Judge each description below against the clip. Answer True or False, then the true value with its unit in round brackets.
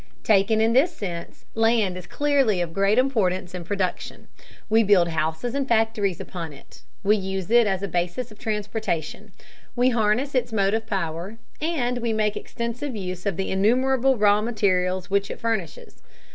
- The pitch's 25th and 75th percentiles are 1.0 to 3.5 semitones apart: False (4.1 semitones)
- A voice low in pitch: False (210 Hz)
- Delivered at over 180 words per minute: False (165 wpm)